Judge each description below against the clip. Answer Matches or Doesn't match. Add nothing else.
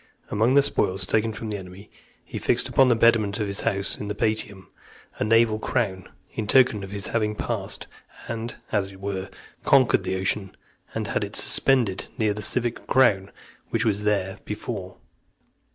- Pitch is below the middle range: Matches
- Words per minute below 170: Doesn't match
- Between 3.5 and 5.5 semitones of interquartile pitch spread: Doesn't match